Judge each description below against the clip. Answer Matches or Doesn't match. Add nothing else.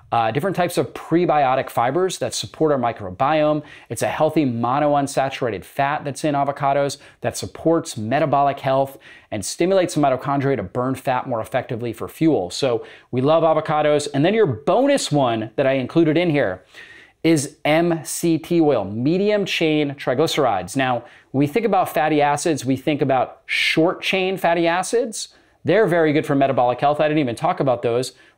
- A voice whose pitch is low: Doesn't match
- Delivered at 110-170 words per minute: Matches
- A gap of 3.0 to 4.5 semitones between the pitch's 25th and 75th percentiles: Matches